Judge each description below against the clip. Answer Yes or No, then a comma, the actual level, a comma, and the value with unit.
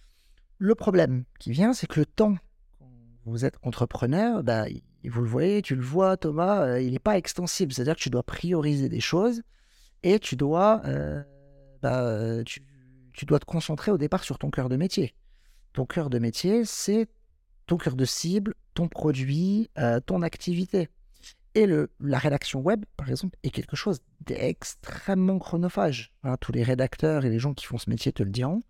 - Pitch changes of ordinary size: No, wide, 6.9 semitones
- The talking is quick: No, average, 180 wpm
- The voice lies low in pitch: No, medium, 145 Hz